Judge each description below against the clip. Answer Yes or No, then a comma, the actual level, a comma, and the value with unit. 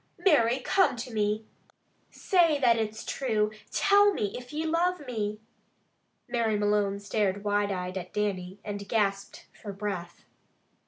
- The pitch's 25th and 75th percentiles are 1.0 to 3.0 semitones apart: No, average, 3.7 semitones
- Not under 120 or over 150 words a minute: Yes, average, 140 wpm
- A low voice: No, high, 210 Hz